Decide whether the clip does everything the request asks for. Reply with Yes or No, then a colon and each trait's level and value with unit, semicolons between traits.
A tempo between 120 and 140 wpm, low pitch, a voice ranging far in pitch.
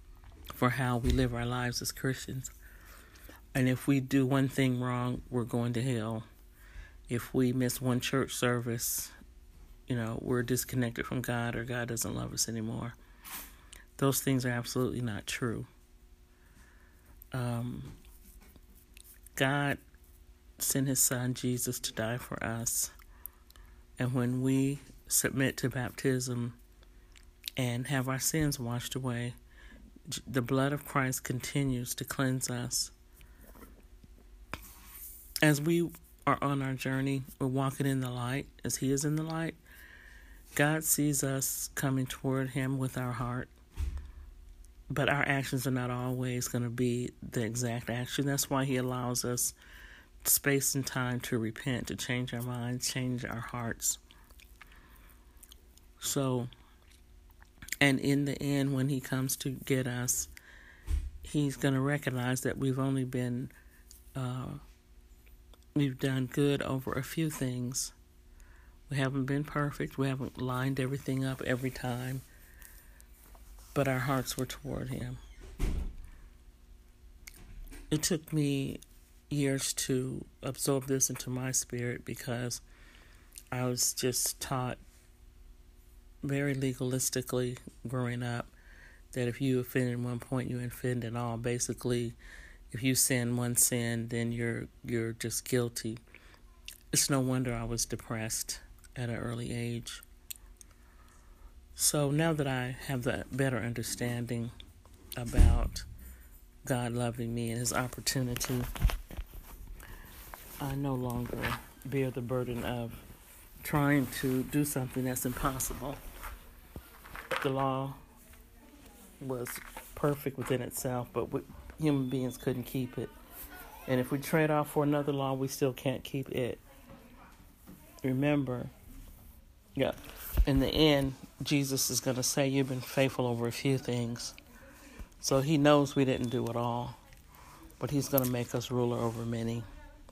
Yes: slow, 135 wpm; low, 125 Hz; wide, 6.5 semitones